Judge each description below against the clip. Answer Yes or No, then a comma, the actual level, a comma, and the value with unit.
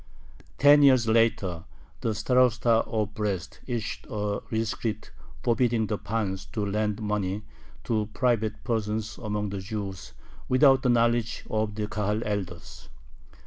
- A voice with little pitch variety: Yes, narrow, 2.0 semitones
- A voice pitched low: Yes, low, 110 Hz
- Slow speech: Yes, slow, 130 wpm